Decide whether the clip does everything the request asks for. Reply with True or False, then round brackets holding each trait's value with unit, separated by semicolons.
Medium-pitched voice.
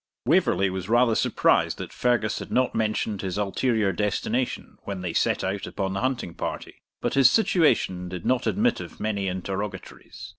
False (105 Hz)